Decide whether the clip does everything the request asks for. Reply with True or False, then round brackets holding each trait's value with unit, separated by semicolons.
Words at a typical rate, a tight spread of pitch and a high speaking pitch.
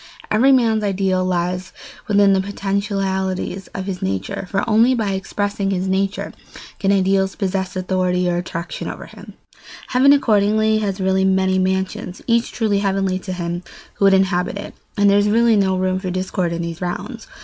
True (170 wpm; 1.7 semitones; 195 Hz)